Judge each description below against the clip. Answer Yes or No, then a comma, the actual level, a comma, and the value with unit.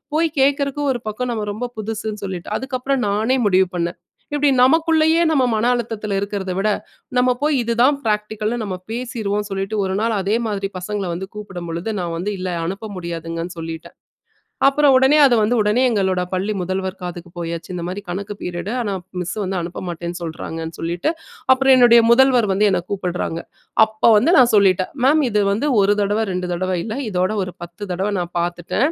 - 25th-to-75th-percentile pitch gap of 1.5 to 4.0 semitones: No, average, 4.8 semitones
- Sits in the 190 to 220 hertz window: Yes, high, 205 Hz